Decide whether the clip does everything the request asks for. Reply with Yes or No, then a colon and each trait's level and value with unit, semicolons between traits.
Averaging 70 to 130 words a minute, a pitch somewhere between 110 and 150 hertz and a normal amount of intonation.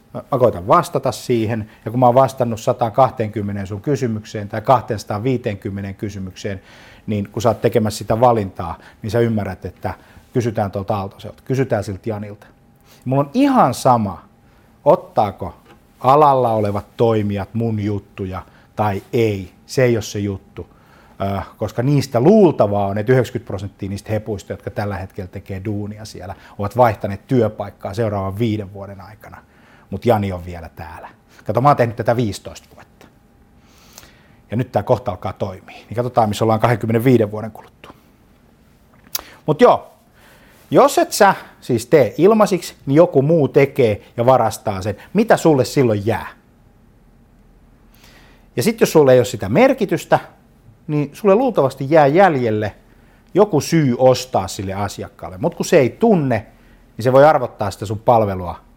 No: average, 150 wpm; low, 115 Hz; average, 3.9 semitones